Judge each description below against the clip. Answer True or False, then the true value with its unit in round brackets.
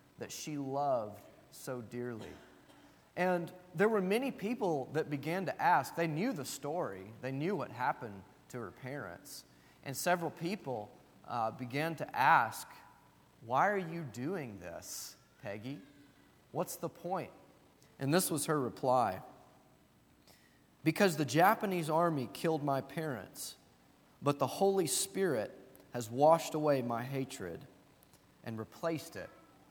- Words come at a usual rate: False (130 wpm)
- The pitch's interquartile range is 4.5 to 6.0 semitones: True (5.6 semitones)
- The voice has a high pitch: False (150 Hz)